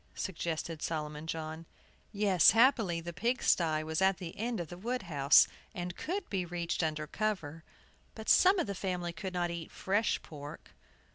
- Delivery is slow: No, average, 165 wpm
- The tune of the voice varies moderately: Yes, average, 4.0 semitones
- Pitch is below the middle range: No, medium, 175 Hz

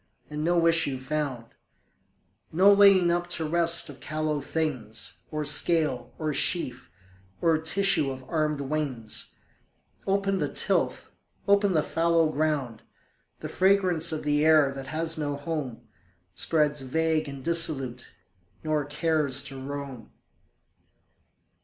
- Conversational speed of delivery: No, slow, 125 wpm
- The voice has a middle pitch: Yes, medium, 155 Hz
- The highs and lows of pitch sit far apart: No, average, 3.2 semitones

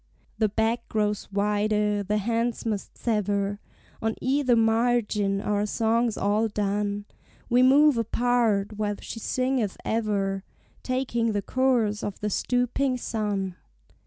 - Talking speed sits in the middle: No, slow, 125 wpm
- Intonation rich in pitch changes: No, narrow, 2.6 semitones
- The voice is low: No, high, 215 Hz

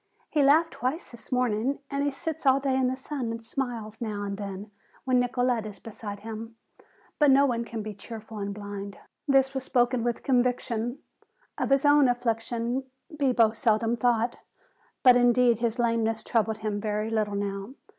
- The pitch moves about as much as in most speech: Yes, average, 3.1 semitones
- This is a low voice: No, high, 235 Hz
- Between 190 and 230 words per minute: No, average, 175 wpm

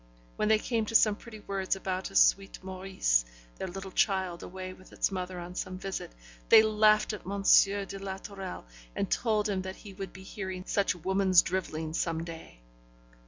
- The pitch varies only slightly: Yes, narrow, 1.6 semitones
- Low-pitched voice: No, high, 190 Hz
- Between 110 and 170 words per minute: No, average, 185 wpm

